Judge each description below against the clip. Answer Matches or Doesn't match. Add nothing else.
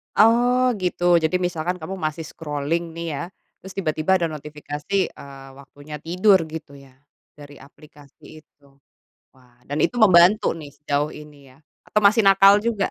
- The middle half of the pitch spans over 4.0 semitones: Matches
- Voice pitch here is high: Doesn't match